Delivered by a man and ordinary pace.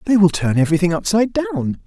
Yes: male; average, 195 wpm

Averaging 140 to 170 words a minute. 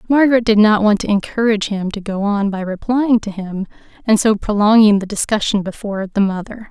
No: average, 195 wpm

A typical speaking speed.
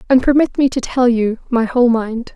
No: fast, 230 wpm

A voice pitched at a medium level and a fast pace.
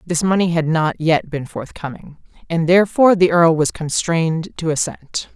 No: medium, 165 Hz; average, 170 wpm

